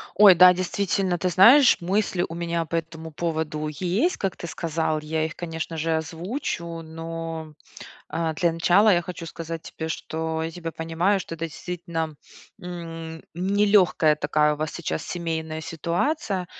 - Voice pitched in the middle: Yes, medium, 165 Hz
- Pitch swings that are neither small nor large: No, narrow, 2.0 semitones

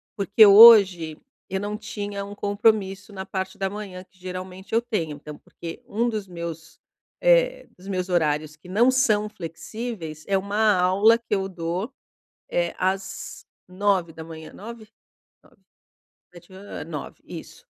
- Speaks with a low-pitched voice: No, high, 195 Hz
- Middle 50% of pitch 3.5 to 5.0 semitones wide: No, average, 3.1 semitones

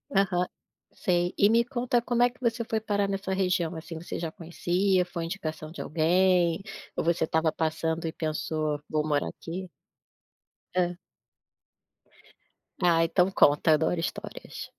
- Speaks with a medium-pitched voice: Yes, medium, 175 Hz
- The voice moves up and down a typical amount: Yes, average, 3.2 semitones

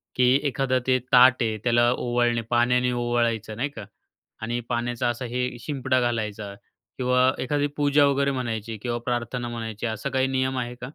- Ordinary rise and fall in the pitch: No, narrow, 1.5 semitones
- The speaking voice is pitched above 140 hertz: No, low, 120 Hz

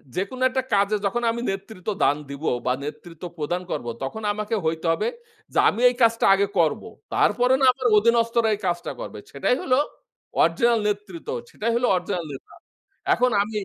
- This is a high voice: Yes, high, 205 Hz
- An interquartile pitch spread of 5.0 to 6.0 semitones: Yes, average, 5.3 semitones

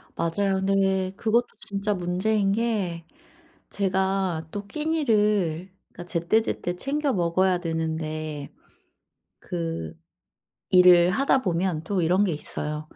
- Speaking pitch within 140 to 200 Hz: Yes, medium, 185 Hz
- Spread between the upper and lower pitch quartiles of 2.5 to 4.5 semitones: Yes, average, 3.4 semitones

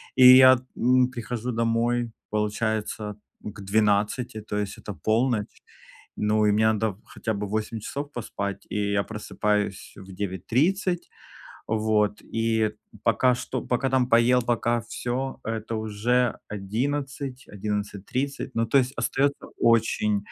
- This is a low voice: Yes, low, 110 Hz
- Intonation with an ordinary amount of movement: Yes, average, 3.1 semitones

